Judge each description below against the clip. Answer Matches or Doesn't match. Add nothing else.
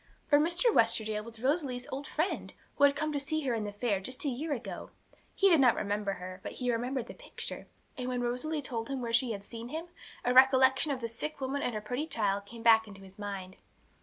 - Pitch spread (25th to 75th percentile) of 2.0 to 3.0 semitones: Doesn't match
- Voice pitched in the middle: Doesn't match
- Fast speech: Matches